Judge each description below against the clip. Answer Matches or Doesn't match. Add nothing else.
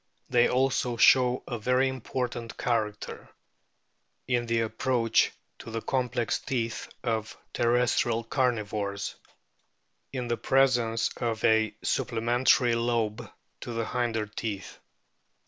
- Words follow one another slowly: Matches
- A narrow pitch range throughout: Matches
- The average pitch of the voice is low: Matches